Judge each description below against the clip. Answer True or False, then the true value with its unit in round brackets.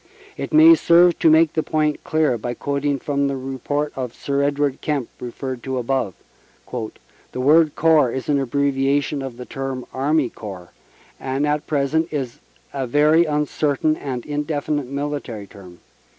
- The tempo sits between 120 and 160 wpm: True (155 wpm)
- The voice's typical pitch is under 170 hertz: True (140 Hz)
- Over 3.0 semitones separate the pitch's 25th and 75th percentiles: False (2.6 semitones)